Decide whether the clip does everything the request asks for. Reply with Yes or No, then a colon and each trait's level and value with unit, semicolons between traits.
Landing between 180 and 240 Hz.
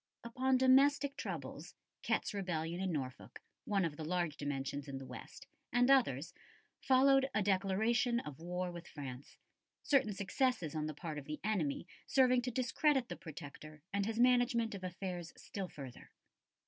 Yes: high, 190 Hz